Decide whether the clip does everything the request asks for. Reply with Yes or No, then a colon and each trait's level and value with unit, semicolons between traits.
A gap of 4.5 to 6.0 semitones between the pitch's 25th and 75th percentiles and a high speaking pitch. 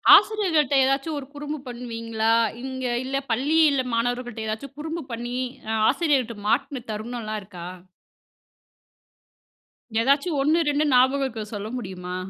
No: average, 4.1 semitones; very high, 255 Hz